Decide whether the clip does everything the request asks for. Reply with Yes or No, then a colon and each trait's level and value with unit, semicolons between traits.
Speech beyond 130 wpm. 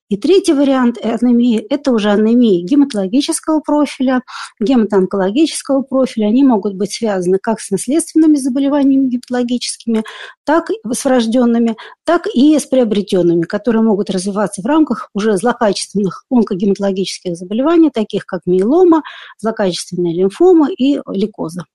No: average, 120 wpm